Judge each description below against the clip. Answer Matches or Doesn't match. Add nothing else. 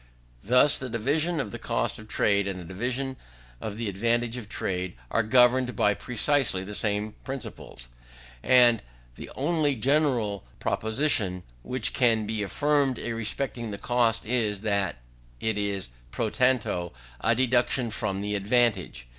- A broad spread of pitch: Doesn't match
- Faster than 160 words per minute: Doesn't match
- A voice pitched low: Matches